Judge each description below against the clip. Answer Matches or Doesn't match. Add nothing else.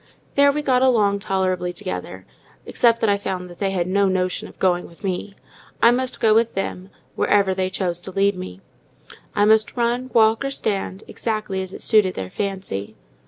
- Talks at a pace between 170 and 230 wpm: Matches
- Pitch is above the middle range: Matches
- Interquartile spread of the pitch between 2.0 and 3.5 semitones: Matches